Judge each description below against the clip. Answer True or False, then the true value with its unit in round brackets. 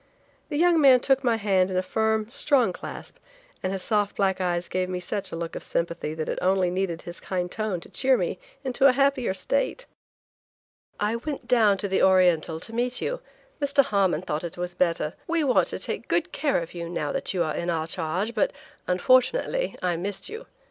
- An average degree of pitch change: False (6.4 semitones)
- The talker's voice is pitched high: True (195 Hz)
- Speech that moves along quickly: True (210 wpm)